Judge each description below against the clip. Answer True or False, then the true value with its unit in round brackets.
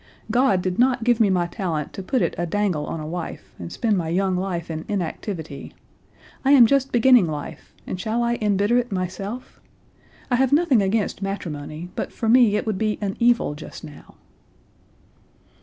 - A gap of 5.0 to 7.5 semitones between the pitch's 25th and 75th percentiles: True (5.4 semitones)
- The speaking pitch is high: True (200 Hz)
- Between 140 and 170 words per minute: False (185 wpm)